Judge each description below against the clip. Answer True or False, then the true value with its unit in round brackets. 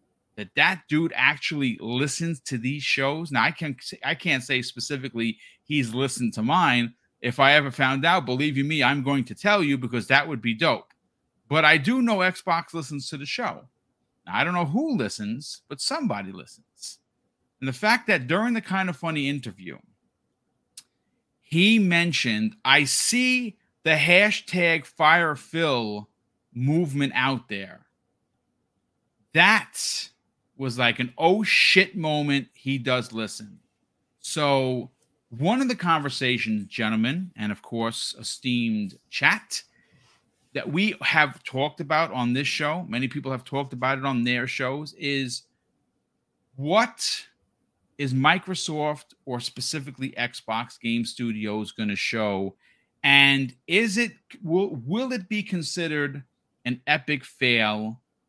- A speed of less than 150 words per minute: True (140 wpm)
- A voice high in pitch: False (140 Hz)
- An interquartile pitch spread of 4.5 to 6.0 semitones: True (5.2 semitones)